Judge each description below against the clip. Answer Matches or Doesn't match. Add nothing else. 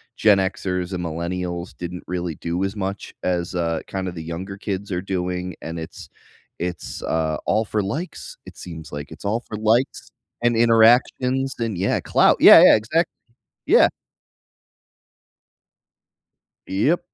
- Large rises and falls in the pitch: Doesn't match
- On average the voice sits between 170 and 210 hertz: Doesn't match